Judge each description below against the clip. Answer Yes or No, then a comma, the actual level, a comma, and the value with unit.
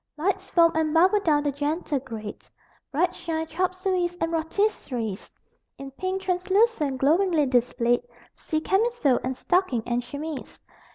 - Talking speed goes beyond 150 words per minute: No, slow, 135 wpm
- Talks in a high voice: Yes, very high, 320 Hz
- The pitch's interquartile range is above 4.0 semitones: Yes, average, 5.3 semitones